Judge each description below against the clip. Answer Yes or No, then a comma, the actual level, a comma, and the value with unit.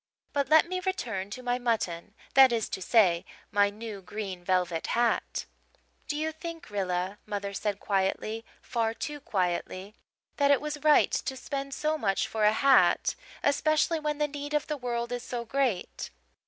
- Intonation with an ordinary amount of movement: No, wide, 6.3 semitones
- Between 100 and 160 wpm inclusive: No, average, 170 wpm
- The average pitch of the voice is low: No, high, 235 Hz